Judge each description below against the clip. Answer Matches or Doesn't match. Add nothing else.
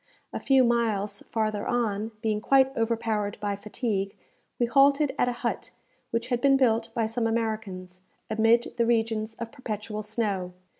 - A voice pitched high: Matches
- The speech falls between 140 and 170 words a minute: Matches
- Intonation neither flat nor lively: Doesn't match